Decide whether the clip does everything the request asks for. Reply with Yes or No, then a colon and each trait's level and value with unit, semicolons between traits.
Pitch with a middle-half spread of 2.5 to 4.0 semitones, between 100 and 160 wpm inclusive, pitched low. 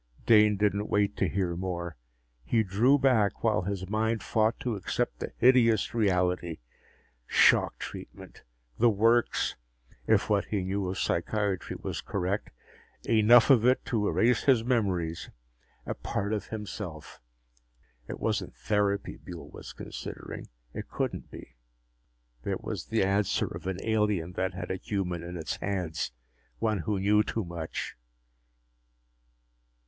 Yes: average, 3.4 semitones; average, 140 wpm; low, 100 Hz